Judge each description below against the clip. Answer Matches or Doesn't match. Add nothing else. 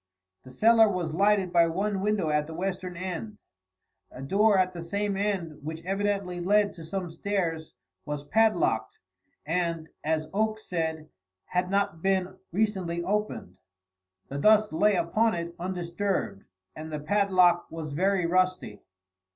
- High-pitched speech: Doesn't match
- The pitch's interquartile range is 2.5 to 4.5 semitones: Matches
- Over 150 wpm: Doesn't match